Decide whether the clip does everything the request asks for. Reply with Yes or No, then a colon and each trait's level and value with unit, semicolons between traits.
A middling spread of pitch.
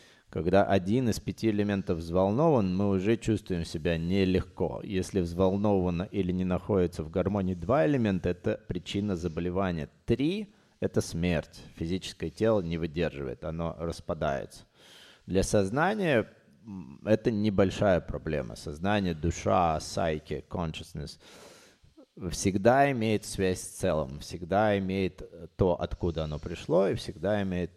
Yes: average, 3.2 semitones